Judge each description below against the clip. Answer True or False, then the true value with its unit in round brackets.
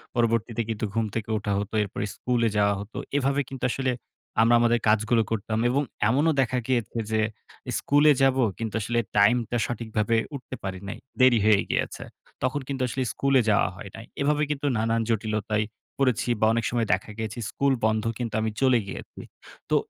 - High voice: False (115 Hz)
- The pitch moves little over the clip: False (3.0 semitones)